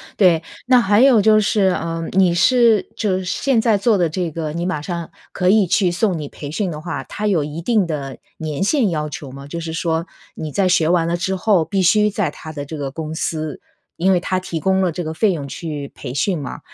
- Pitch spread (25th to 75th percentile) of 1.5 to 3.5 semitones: No, average, 4.0 semitones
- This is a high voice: No, medium, 175 Hz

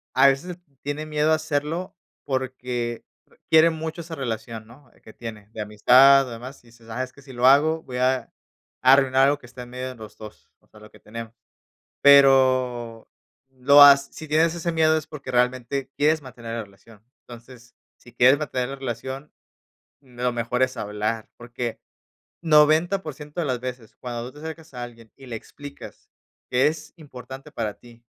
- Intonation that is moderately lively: Yes, average, 3.4 semitones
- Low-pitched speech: Yes, low, 130 Hz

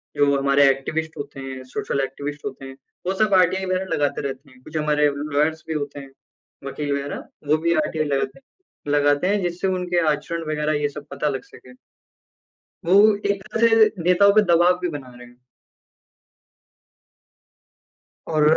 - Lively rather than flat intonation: No, average, 4.1 semitones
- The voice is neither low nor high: Yes, medium, 150 Hz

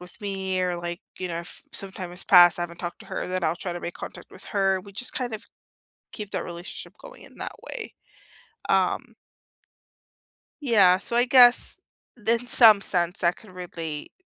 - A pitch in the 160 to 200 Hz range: Yes, medium, 185 Hz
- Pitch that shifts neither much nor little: Yes, average, 3.7 semitones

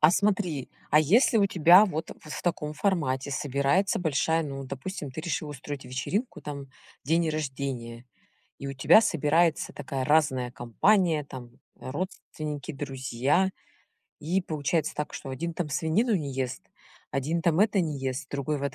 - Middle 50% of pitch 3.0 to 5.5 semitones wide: Yes, average, 3.9 semitones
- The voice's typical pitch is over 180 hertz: No, medium, 150 Hz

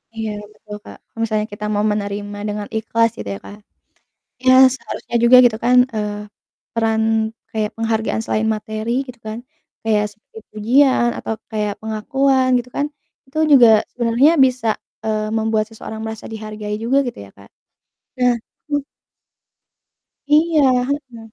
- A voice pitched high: Yes, high, 220 Hz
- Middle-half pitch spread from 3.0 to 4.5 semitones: No, narrow, 2.5 semitones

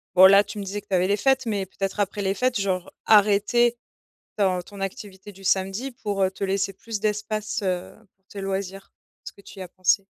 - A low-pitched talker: No, high, 200 Hz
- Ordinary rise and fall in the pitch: No, narrow, 1.5 semitones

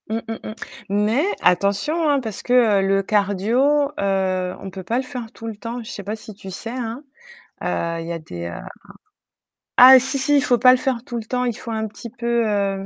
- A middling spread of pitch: Yes, average, 4.2 semitones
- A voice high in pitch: Yes, high, 225 Hz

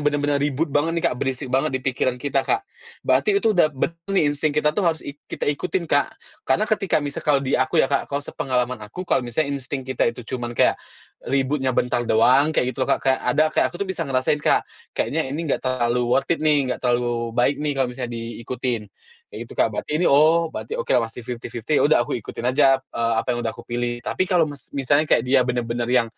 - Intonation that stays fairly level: No, average, 3.8 semitones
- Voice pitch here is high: No, low, 135 Hz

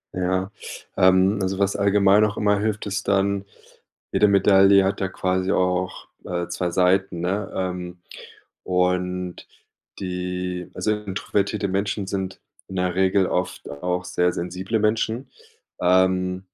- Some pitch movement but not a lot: No, narrow, 1.6 semitones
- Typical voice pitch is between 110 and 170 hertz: No, very low, 95 Hz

